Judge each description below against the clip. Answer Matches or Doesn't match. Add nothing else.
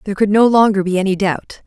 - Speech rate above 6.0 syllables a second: Matches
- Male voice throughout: Doesn't match